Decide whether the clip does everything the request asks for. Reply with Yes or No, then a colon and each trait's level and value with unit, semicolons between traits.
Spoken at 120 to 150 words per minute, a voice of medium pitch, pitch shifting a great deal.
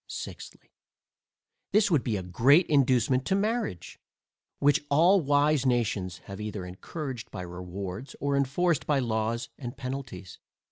No: slow, 135 wpm; low, 130 Hz; wide, 5.8 semitones